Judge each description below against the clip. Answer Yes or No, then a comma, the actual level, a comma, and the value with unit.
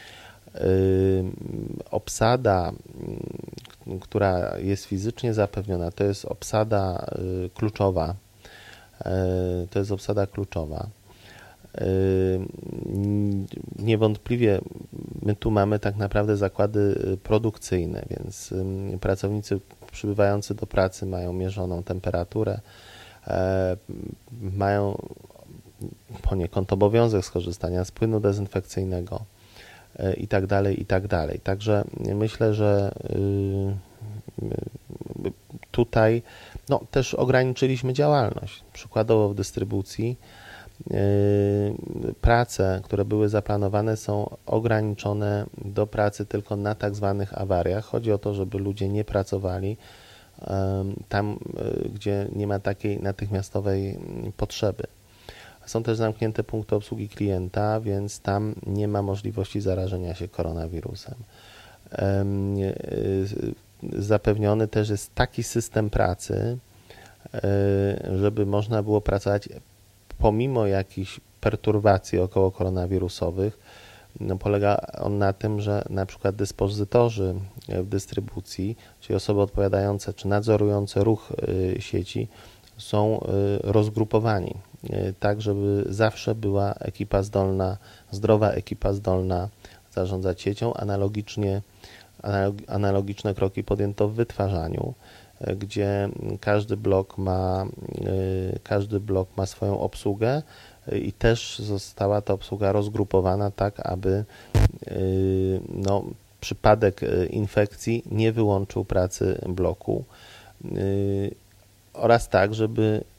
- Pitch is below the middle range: Yes, low, 100 Hz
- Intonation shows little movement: Yes, narrow, 1.9 semitones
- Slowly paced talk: Yes, slow, 90 wpm